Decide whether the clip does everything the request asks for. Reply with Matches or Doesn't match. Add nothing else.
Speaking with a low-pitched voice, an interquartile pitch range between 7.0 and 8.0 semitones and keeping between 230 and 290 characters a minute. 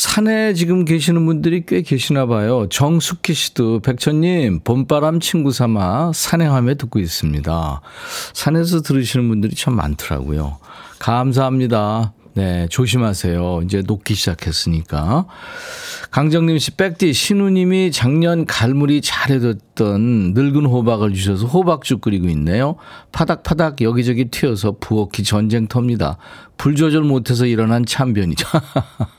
Doesn't match